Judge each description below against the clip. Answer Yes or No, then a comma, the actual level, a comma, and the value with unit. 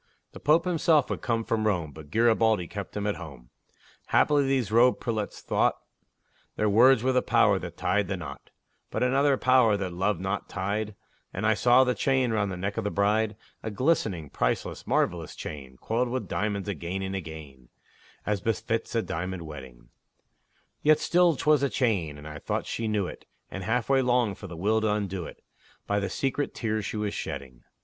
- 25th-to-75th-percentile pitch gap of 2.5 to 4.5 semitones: No, average, 5.2 semitones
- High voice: No, low, 105 Hz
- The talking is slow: No, average, 190 wpm